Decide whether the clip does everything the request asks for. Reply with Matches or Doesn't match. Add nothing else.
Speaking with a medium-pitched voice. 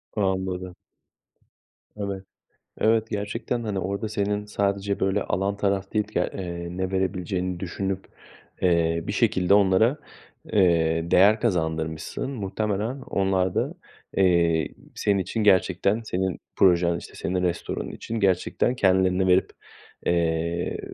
Doesn't match